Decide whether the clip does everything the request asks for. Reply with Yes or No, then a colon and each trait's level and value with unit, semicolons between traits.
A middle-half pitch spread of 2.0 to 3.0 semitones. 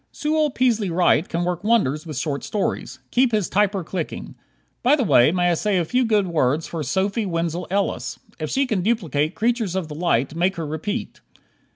No: average, 5.0 semitones